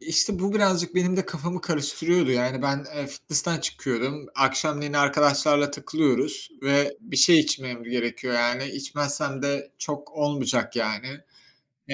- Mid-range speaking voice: Yes, medium, 145 Hz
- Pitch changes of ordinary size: Yes, average, 3.2 semitones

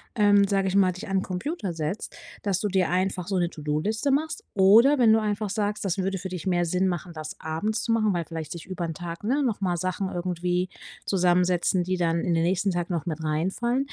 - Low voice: No, medium, 185 Hz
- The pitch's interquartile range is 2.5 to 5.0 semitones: Yes, average, 2.9 semitones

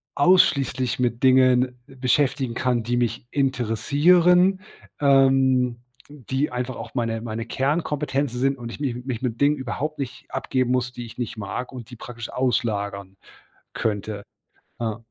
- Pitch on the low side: Yes, low, 125 Hz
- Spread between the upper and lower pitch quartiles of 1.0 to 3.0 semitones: Yes, narrow, 2.5 semitones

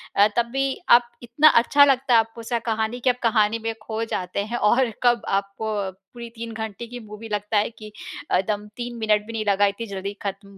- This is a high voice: Yes, high, 225 Hz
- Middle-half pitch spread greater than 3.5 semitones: No, narrow, 2.5 semitones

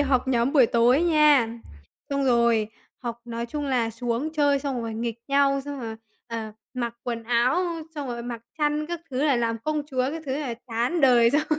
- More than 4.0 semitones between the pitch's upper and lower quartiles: No, average, 3.7 semitones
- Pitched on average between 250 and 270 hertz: Yes, very high, 255 Hz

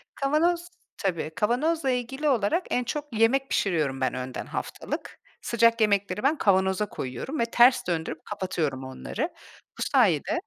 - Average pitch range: No, wide, 7.9 semitones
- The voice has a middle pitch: No, high, 220 Hz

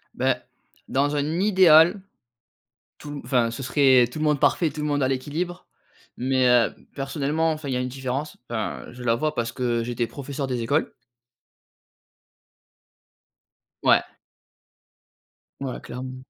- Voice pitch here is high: No, low, 135 Hz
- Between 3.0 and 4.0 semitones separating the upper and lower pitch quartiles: Yes, average, 3.4 semitones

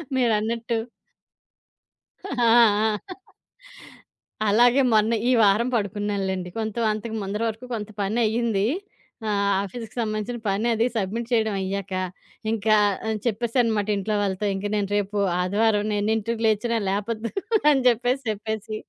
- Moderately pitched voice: No, high, 215 Hz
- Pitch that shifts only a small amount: Yes, narrow, 2.2 semitones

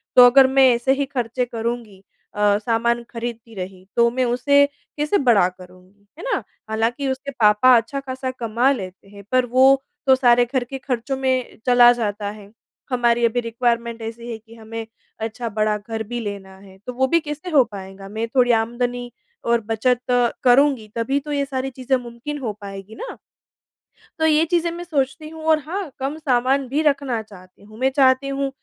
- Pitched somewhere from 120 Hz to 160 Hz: No, high, 245 Hz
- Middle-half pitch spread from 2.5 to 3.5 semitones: Yes, average, 3.2 semitones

